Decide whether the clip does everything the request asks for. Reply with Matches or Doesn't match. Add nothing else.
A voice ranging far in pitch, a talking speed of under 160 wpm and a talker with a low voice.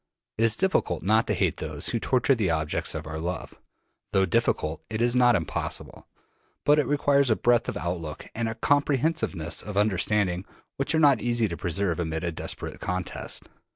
Doesn't match